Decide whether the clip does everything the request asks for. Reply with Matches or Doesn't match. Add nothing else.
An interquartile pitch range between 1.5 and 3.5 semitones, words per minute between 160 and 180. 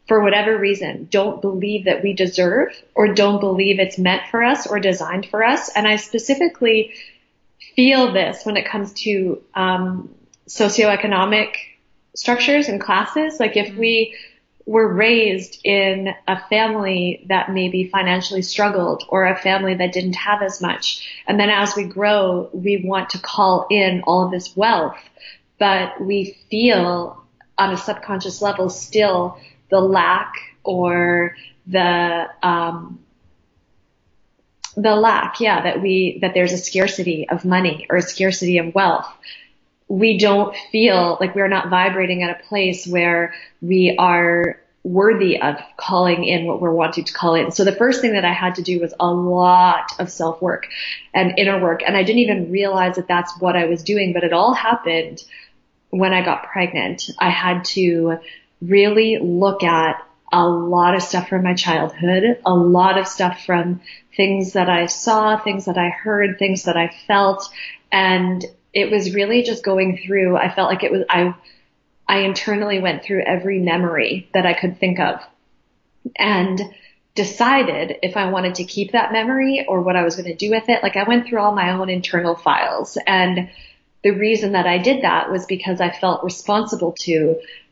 Matches